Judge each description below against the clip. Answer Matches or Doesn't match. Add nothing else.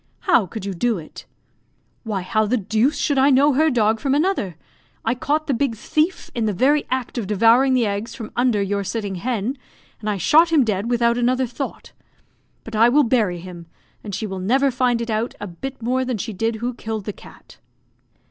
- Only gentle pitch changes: Doesn't match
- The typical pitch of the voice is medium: Doesn't match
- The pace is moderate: Doesn't match